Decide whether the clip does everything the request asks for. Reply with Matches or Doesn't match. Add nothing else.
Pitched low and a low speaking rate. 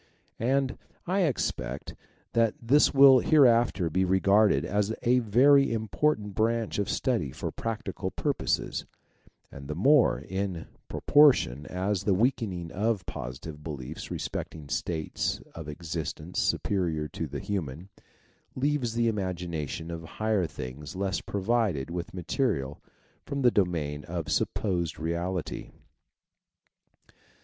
Matches